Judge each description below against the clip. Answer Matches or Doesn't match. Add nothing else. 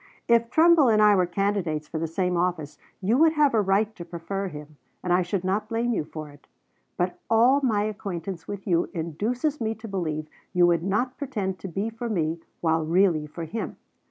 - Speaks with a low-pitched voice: Doesn't match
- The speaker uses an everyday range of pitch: Matches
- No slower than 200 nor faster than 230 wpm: Matches